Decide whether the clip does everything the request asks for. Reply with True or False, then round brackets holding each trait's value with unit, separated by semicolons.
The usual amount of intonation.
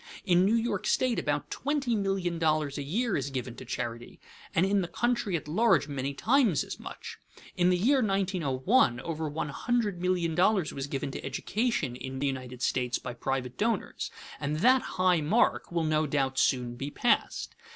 False (7.0 semitones)